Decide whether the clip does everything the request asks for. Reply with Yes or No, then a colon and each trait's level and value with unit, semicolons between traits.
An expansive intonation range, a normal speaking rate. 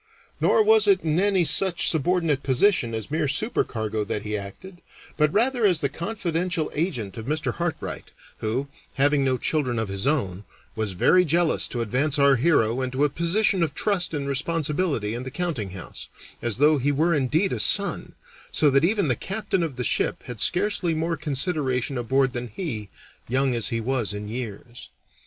Yes: wide, 6.1 semitones; average, 180 wpm